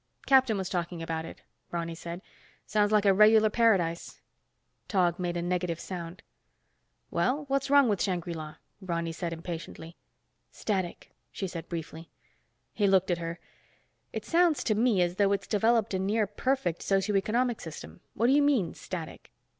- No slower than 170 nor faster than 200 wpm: No, average, 160 wpm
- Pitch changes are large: No, average, 4.2 semitones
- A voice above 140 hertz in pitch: Yes, high, 190 Hz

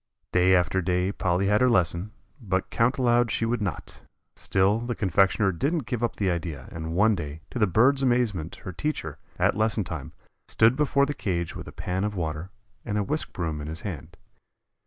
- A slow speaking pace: No, average, 200 wpm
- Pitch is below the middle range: Yes, very low, 95 Hz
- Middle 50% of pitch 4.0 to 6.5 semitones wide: Yes, average, 5.2 semitones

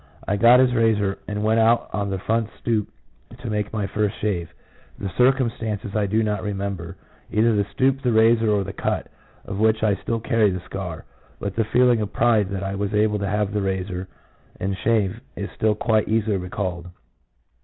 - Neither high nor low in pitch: No, low, 105 Hz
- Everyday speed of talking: Yes, average, 195 wpm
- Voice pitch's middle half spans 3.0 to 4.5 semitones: No, narrow, 2.4 semitones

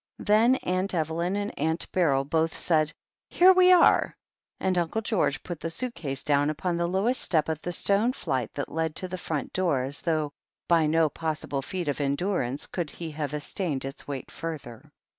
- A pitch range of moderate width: Yes, average, 4.1 semitones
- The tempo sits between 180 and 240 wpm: Yes, average, 195 wpm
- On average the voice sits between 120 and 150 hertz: No, medium, 165 Hz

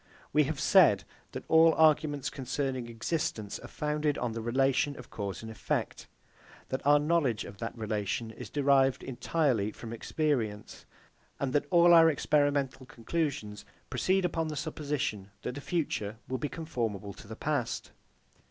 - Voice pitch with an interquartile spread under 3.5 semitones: No, average, 5.0 semitones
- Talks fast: No, average, 150 wpm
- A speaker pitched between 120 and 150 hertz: Yes, low, 135 Hz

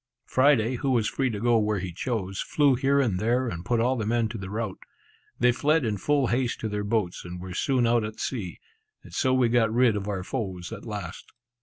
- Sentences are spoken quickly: Yes, fast, 230 wpm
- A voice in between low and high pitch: No, low, 115 Hz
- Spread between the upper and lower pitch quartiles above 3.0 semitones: Yes, average, 3.7 semitones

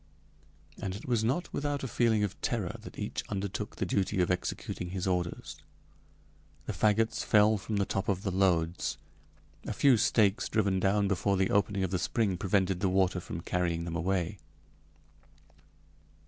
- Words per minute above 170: No, average, 165 wpm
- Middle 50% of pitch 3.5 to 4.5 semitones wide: No, narrow, 2.4 semitones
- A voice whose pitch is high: No, very low, 95 Hz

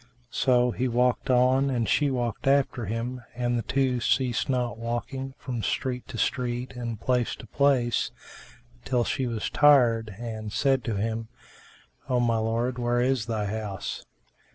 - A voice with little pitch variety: Yes, narrow, 2.1 semitones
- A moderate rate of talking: Yes, average, 155 wpm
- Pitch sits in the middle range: No, low, 120 Hz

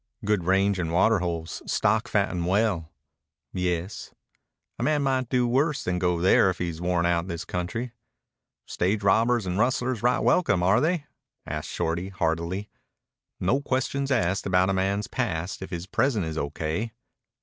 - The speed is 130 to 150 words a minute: No, average, 160 wpm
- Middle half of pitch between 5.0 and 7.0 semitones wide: Yes, average, 5.3 semitones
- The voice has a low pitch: Yes, very low, 95 Hz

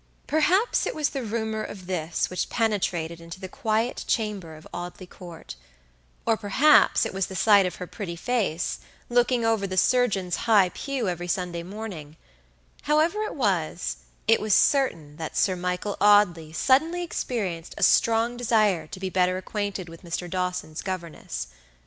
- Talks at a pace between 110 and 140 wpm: No, average, 160 wpm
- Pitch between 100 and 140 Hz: No, high, 190 Hz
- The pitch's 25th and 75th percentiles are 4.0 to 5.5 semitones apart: Yes, average, 4.5 semitones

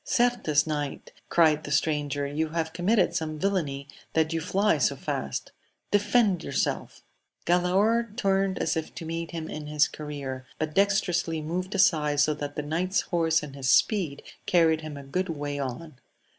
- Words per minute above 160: Yes, average, 170 wpm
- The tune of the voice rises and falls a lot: No, average, 3.8 semitones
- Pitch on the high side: No, medium, 160 Hz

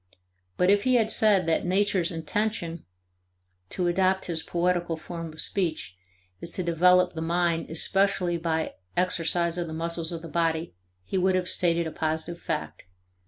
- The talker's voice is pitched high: No, medium, 170 Hz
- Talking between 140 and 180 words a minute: Yes, average, 165 wpm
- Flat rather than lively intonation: Yes, narrow, 1.9 semitones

